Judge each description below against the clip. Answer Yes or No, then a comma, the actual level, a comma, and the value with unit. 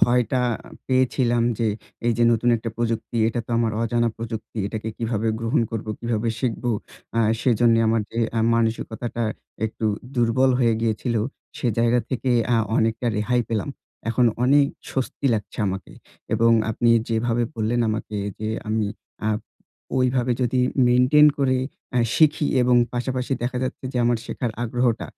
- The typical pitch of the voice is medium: No, low, 120 Hz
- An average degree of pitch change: No, narrow, 1.8 semitones